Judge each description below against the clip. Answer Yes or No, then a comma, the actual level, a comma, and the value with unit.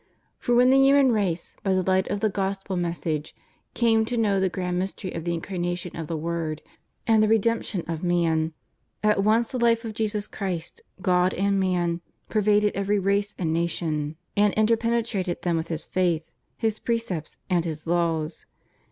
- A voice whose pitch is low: No, high, 190 Hz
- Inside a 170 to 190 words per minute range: Yes, average, 175 wpm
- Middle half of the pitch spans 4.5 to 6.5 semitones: No, average, 4.0 semitones